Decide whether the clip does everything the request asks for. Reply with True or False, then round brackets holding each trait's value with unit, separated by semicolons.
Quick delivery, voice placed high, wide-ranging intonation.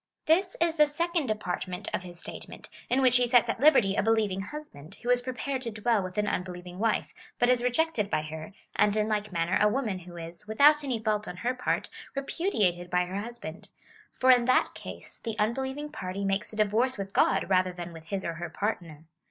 True (220 wpm; 215 Hz; 5.7 semitones)